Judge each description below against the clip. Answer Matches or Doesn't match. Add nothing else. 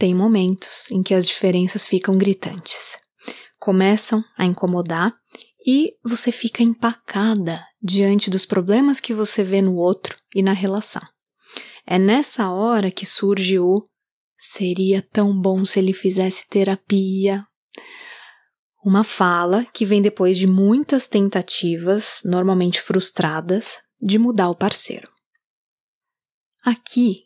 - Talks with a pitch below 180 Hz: Doesn't match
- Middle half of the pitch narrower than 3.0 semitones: Matches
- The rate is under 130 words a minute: Matches